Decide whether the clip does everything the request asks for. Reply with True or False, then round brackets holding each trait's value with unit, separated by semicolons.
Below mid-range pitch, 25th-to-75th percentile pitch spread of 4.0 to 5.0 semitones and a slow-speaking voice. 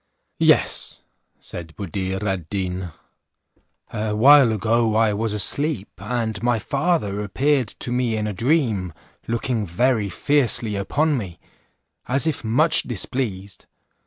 True (110 Hz; 4.3 semitones; 125 wpm)